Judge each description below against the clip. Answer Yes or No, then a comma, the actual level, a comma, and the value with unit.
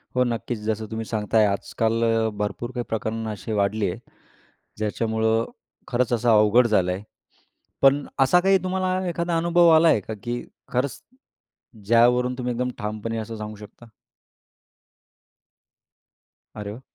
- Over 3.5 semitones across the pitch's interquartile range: No, average, 2.8 semitones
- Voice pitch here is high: No, low, 115 Hz